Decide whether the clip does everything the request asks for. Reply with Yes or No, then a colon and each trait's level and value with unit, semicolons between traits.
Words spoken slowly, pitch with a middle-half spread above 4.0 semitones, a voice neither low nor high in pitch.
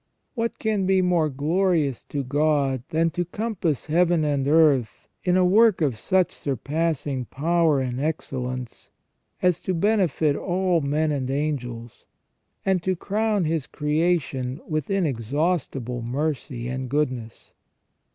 Yes: slow, 130 wpm; average, 5.0 semitones; medium, 155 Hz